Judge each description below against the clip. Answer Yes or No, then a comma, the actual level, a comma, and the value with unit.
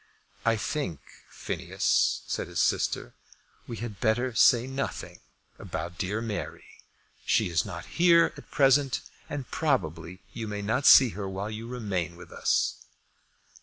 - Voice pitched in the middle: No, low, 110 Hz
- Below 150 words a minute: Yes, average, 140 wpm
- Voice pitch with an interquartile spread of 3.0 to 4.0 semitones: No, average, 5.1 semitones